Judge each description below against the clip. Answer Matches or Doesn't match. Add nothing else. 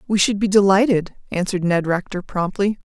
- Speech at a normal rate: Matches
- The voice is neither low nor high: Doesn't match